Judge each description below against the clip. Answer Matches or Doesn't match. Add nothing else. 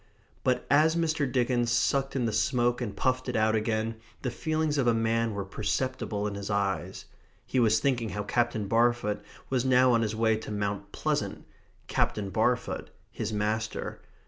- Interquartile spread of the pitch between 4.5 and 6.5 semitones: Doesn't match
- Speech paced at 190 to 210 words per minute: Doesn't match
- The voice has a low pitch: Matches